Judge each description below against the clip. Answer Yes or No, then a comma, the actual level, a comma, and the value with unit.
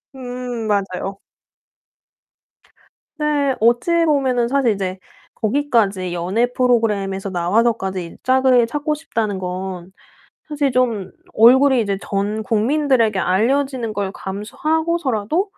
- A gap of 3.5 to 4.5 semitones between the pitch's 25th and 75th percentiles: No, average, 5.2 semitones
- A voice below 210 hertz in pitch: No, high, 230 Hz